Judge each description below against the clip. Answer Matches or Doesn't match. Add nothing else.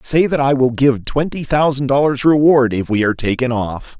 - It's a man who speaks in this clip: Matches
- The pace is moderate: Doesn't match